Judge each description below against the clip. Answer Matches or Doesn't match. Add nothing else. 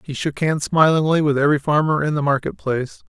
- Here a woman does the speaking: Doesn't match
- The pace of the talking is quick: Matches